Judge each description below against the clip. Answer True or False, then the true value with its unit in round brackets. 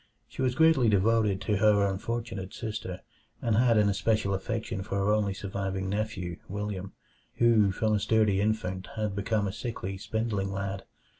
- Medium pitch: False (105 Hz)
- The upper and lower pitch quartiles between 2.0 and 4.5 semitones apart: True (2.4 semitones)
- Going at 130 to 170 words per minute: True (160 wpm)